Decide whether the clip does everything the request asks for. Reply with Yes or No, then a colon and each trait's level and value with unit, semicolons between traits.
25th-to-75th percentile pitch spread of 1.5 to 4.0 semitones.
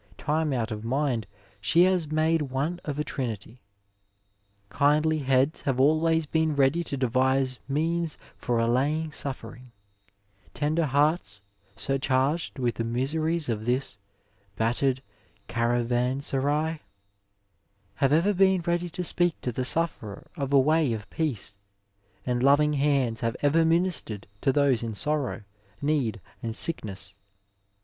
No: average, 4.5 semitones